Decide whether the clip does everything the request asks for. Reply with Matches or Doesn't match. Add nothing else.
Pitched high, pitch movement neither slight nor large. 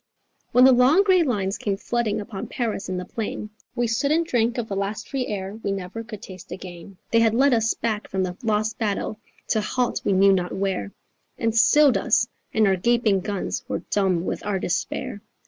Matches